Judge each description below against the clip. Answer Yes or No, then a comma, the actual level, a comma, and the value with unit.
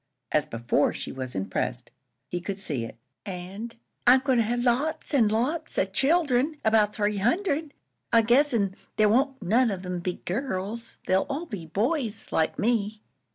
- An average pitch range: No, wide, 5.8 semitones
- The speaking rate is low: No, average, 170 wpm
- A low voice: No, high, 220 Hz